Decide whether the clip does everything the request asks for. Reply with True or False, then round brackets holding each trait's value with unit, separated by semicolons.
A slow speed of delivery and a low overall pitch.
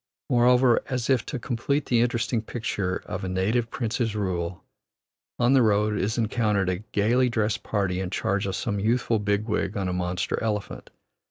False (175 wpm; 110 Hz)